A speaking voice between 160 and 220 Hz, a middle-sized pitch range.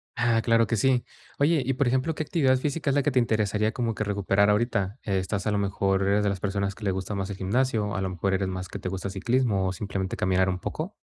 No: low, 105 Hz; average, 4.2 semitones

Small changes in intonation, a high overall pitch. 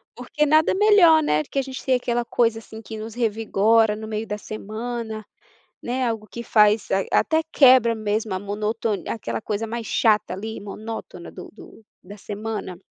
Yes: narrow, 2.2 semitones; high, 220 Hz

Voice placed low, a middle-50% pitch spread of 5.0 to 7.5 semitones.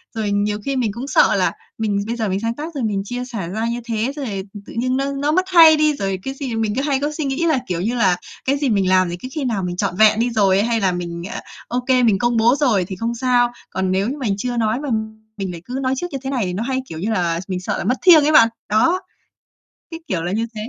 No: high, 230 Hz; average, 5.3 semitones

